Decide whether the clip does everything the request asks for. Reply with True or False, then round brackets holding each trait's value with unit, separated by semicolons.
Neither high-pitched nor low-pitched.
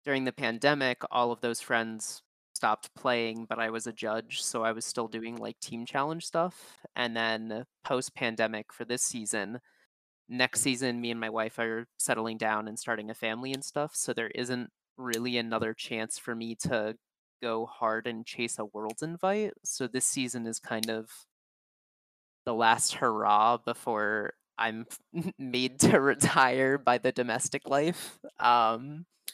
False (120 Hz)